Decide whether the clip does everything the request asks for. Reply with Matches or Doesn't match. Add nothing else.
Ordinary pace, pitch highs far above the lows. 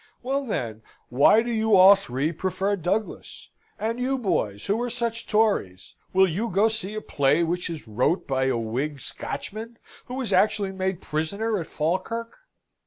Matches